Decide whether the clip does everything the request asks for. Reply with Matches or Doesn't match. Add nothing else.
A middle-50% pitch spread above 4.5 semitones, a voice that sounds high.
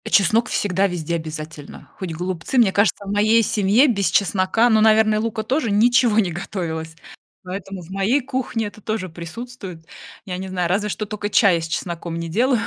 Doesn't match